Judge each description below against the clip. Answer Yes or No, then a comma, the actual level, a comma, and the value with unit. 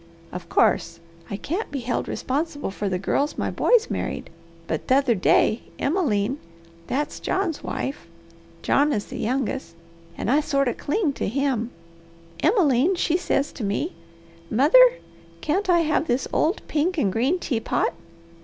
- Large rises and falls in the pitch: Yes, wide, 5.9 semitones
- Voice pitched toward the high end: Yes, very high, 280 Hz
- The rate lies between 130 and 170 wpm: Yes, average, 150 wpm